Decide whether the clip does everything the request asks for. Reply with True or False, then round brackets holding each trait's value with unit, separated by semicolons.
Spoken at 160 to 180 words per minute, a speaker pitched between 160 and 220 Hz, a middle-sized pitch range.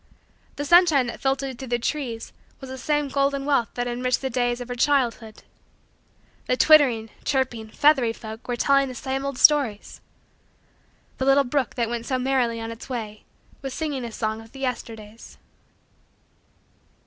False (165 wpm; 255 Hz; 3.0 semitones)